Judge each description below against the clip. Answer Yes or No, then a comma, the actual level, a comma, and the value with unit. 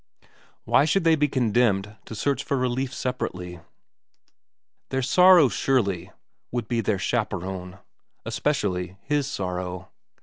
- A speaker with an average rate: No, slow, 125 wpm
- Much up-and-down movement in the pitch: Yes, wide, 6.5 semitones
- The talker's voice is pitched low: Yes, low, 120 Hz